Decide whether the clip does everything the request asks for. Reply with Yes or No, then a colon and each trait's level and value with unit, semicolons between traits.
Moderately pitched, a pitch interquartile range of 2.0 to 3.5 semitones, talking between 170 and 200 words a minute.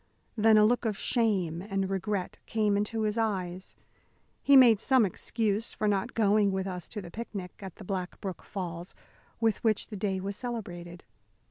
No: high, 205 Hz; average, 2.8 semitones; average, 175 wpm